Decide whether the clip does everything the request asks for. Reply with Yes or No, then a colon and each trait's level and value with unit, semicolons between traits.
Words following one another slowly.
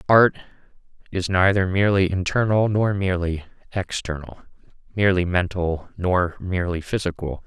Yes: slow, 105 wpm